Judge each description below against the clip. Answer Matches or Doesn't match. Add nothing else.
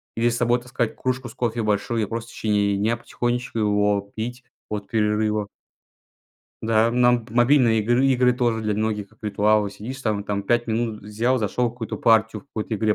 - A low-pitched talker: Matches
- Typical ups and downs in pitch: Doesn't match